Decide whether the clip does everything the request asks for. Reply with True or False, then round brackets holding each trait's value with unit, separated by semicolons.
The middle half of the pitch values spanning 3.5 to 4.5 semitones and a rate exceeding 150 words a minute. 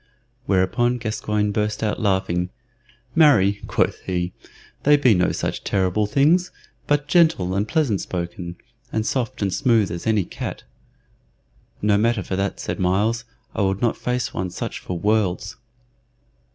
False (4.1 semitones; 145 wpm)